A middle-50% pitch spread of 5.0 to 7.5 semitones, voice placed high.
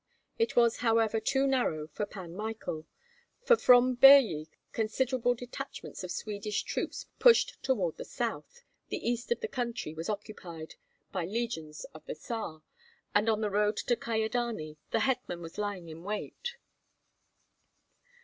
Yes: wide, 5.6 semitones; high, 220 Hz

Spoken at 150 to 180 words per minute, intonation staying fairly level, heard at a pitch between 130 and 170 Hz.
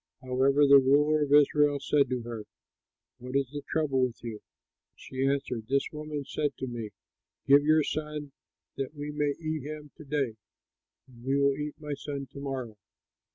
Yes: average, 175 wpm; narrow, 2.1 semitones; medium, 140 Hz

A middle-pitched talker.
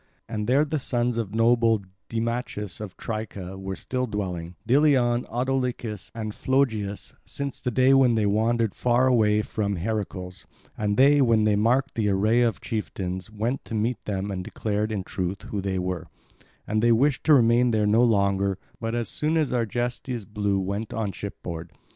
No: low, 110 Hz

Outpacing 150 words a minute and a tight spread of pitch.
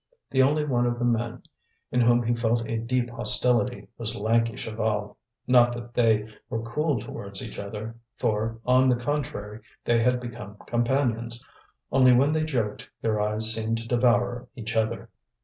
Yes: average, 165 wpm; narrow, 1.8 semitones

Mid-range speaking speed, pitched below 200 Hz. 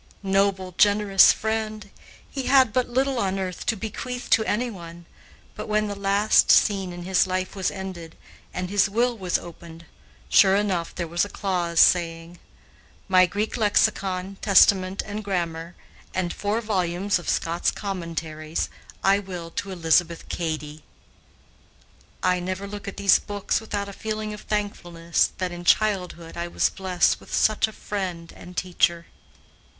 Yes: average, 150 wpm; high, 190 Hz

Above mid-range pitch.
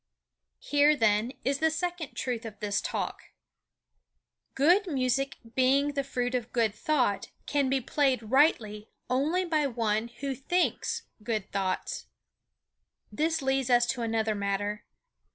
Yes: very high, 255 Hz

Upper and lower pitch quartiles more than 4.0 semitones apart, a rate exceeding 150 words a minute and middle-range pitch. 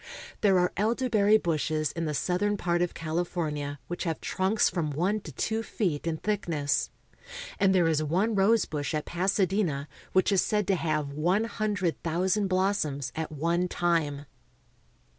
Yes: average, 4.4 semitones; average, 160 wpm; medium, 175 Hz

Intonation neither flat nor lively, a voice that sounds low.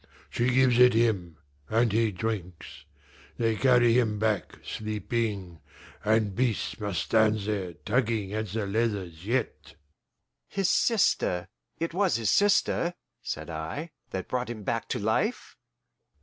Yes: average, 3.5 semitones; low, 110 Hz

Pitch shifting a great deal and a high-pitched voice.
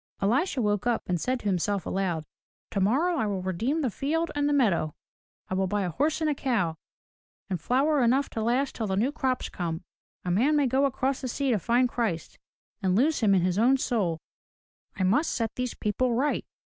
Yes: wide, 6.0 semitones; high, 235 Hz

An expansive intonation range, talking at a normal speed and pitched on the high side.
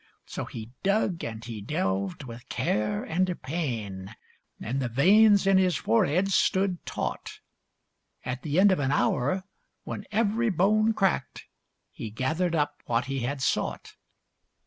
No: wide, 8.3 semitones; average, 145 wpm; medium, 145 Hz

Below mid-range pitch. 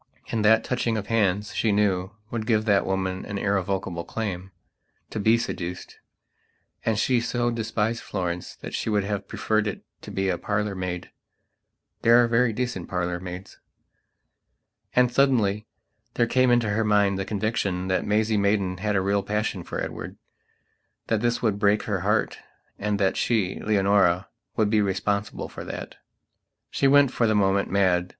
Yes: low, 105 Hz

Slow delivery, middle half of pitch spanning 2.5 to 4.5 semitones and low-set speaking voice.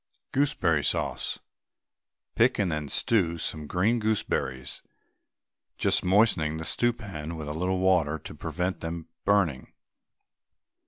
No: slow, 115 wpm; average, 5.0 semitones; very low, 90 Hz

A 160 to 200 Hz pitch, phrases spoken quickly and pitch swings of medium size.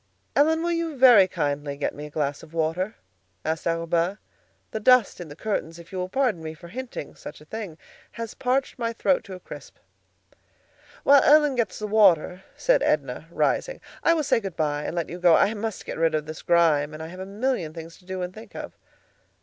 No: medium, 185 Hz; fast, 215 wpm; wide, 6.6 semitones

